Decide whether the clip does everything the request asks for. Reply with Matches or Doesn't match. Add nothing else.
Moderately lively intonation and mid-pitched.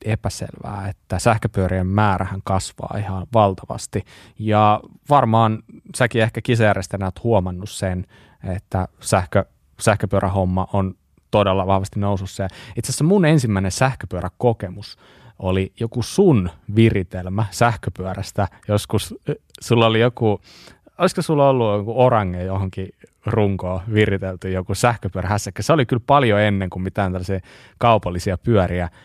Doesn't match